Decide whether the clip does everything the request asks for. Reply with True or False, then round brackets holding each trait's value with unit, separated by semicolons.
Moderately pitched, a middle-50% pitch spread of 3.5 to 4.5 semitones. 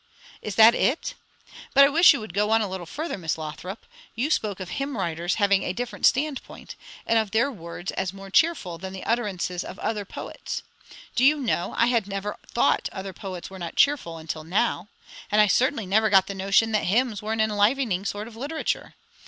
False (210 Hz; 4.1 semitones)